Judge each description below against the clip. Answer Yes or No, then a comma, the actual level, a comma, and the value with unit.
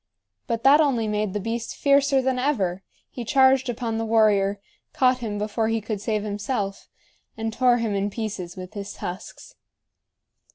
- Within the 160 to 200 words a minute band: Yes, average, 165 wpm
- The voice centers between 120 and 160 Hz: No, high, 225 Hz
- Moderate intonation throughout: Yes, average, 3.6 semitones